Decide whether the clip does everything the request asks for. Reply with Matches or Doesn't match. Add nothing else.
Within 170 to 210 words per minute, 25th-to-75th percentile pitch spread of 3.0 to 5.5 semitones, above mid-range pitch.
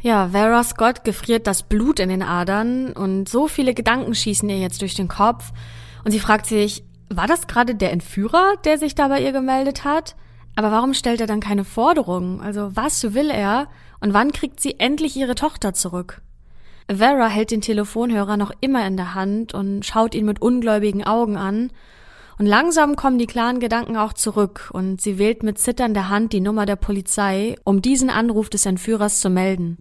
Matches